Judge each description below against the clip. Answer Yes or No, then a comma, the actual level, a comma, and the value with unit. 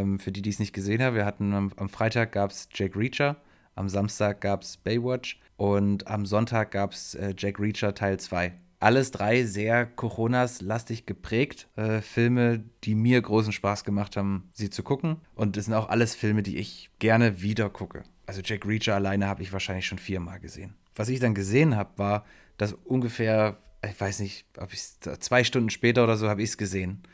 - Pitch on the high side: No, low, 105 Hz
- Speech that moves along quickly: Yes, fast, 200 wpm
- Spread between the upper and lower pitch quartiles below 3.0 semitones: Yes, narrow, 2.6 semitones